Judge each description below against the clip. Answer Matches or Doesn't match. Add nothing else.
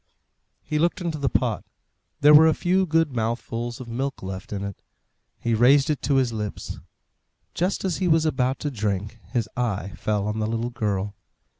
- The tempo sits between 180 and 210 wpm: Matches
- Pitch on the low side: Matches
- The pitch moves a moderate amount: Doesn't match